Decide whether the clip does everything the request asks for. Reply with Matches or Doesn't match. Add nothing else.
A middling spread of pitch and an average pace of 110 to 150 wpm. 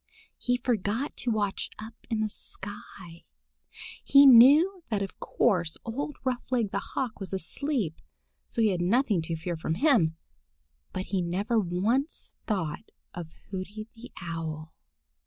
Doesn't match